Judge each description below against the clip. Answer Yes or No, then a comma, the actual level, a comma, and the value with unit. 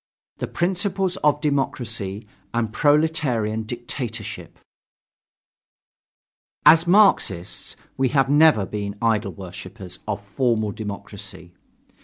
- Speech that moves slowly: Yes, slow, 90 wpm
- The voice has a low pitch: Yes, low, 115 Hz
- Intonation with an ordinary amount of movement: No, wide, 6.4 semitones